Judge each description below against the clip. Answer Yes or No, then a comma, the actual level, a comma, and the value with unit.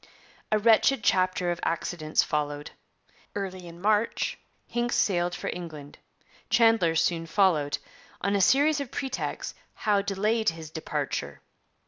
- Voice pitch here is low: No, medium, 185 Hz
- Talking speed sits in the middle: No, slow, 125 wpm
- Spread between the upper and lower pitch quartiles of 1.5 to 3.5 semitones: No, average, 4.9 semitones